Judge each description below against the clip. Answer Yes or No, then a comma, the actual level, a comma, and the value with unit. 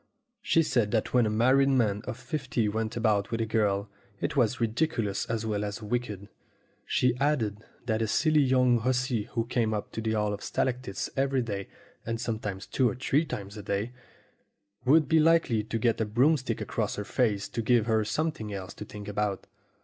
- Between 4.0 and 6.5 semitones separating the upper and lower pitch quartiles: No, average, 3.4 semitones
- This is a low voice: Yes, low, 115 Hz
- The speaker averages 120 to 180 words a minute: No, average, 195 wpm